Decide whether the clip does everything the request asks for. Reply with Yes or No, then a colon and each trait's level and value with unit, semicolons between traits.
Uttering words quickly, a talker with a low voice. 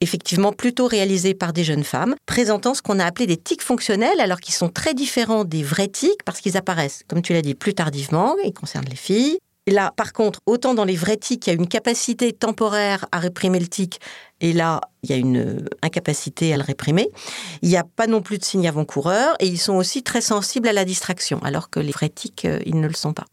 No: fast, 240 wpm; high, 190 Hz